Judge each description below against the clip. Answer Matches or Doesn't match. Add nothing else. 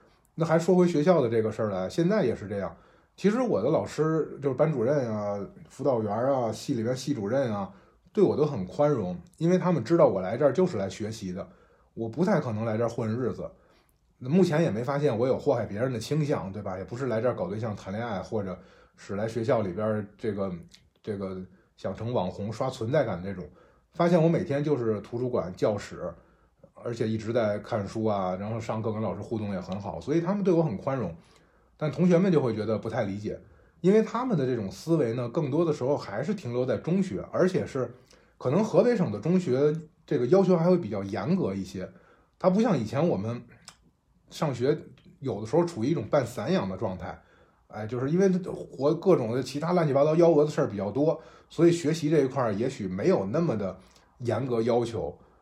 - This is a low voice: Matches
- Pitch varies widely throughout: Matches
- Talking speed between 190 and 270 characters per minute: Doesn't match